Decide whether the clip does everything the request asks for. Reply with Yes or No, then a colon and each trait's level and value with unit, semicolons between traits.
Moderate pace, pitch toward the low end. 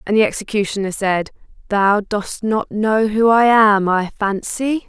No: average, 160 wpm; high, 210 Hz